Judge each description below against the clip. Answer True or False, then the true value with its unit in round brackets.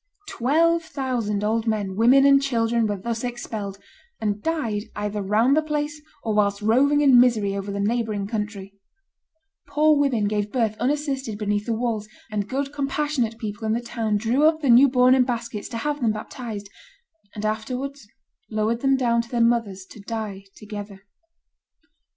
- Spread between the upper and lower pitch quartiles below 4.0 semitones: False (4.3 semitones)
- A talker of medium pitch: False (230 Hz)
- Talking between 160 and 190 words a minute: True (170 wpm)